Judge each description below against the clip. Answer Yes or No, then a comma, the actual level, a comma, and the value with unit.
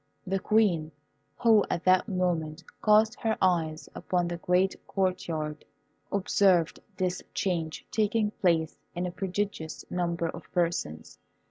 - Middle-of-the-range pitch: Yes, medium, 180 Hz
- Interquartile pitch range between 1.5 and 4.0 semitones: Yes, average, 2.9 semitones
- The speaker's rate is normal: No, slow, 130 wpm